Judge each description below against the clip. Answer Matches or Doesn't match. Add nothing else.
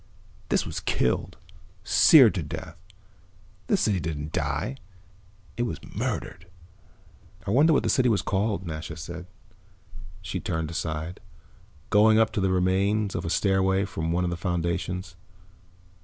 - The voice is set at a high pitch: Doesn't match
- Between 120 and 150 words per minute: Matches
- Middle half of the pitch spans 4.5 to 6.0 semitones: Doesn't match